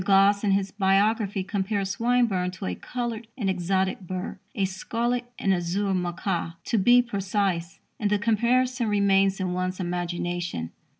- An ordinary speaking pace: Yes, average, 145 wpm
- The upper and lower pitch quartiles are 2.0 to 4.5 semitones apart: Yes, average, 2.7 semitones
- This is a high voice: Yes, high, 195 Hz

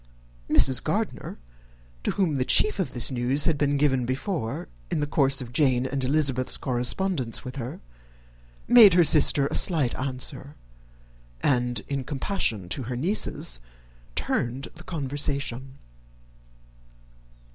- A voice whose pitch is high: No, low, 135 Hz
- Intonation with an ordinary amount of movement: Yes, average, 3.0 semitones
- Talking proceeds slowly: Yes, slow, 130 wpm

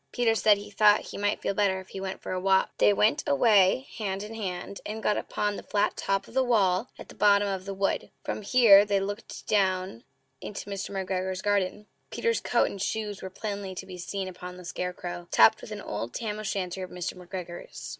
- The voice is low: No, high, 195 Hz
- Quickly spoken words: Yes, fast, 220 wpm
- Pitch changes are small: Yes, narrow, 2.0 semitones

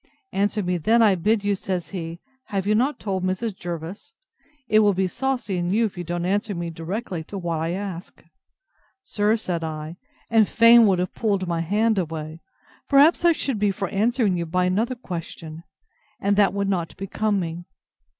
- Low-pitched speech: No, high, 195 Hz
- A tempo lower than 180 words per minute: No, average, 190 wpm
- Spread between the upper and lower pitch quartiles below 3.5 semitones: No, average, 3.8 semitones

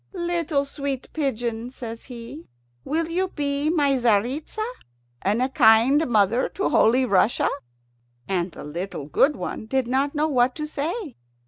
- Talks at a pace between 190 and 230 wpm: No, average, 145 wpm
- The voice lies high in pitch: Yes, very high, 265 Hz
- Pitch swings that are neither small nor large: Yes, average, 4.9 semitones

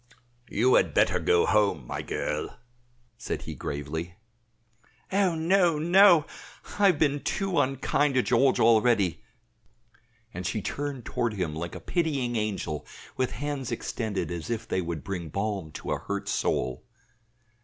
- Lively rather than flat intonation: Yes, wide, 8.4 semitones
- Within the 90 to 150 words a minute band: Yes, average, 145 wpm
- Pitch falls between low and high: No, low, 115 Hz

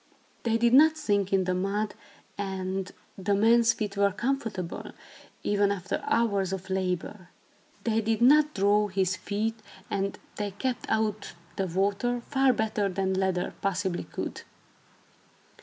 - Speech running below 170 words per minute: Yes, average, 140 wpm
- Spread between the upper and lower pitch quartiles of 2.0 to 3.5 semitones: Yes, average, 2.8 semitones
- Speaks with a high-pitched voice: Yes, high, 200 Hz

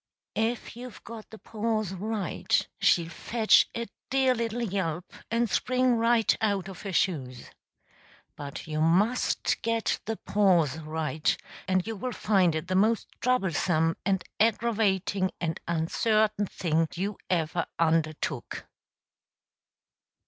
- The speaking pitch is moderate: No, high, 195 Hz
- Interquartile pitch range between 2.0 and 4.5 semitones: No, wide, 5.4 semitones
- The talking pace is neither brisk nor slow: No, slow, 125 wpm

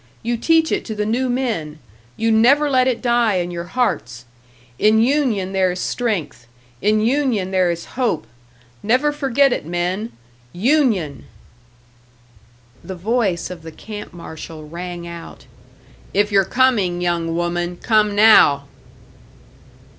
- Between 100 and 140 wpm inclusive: Yes, slow, 135 wpm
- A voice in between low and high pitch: No, high, 205 Hz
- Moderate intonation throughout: No, wide, 5.7 semitones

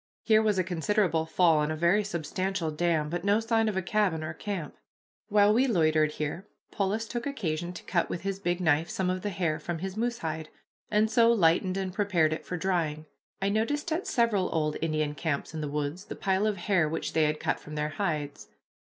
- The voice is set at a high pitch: No, medium, 180 Hz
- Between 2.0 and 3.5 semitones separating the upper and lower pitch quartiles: No, average, 4.7 semitones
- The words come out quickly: Yes, fast, 215 wpm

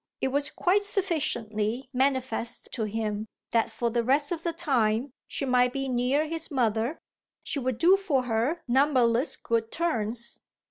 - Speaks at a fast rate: No, average, 155 wpm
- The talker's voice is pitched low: No, very high, 255 Hz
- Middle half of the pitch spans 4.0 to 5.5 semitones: Yes, average, 4.4 semitones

